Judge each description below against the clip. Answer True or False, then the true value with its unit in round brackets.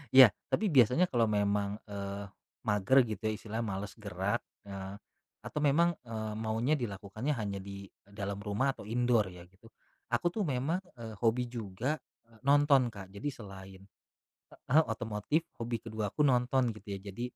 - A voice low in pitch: True (110 Hz)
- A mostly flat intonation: False (3.8 semitones)